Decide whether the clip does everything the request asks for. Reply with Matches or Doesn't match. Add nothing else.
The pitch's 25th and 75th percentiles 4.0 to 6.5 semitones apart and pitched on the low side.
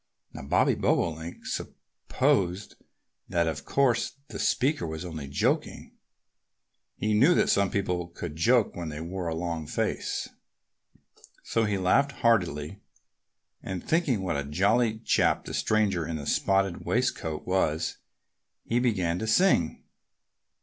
Matches